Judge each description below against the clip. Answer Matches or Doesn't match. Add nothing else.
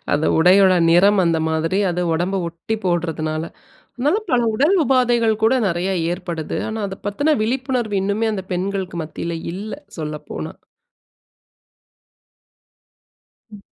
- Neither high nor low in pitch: Doesn't match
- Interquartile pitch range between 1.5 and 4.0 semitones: Doesn't match